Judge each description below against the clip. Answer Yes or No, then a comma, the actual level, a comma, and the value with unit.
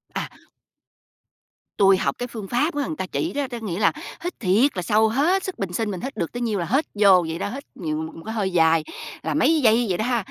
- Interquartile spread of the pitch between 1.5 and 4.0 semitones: No, wide, 5.6 semitones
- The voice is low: No, high, 215 Hz